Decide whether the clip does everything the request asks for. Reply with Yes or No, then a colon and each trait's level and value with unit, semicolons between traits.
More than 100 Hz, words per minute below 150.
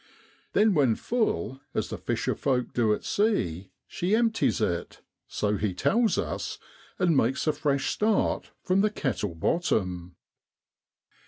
Yes: low, 135 Hz; average, 140 wpm